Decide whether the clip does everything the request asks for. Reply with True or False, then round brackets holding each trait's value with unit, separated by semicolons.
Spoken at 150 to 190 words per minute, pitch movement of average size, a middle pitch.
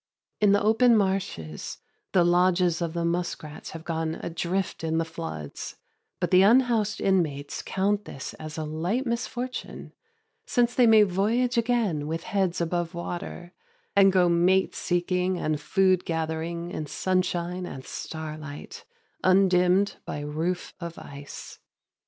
False (135 wpm; 3.3 semitones; 180 Hz)